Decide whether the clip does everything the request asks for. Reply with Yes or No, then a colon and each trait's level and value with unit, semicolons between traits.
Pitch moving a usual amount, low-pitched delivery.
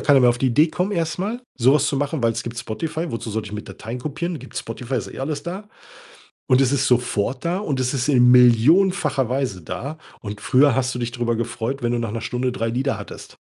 Yes: average, 4.0 semitones; low, 130 Hz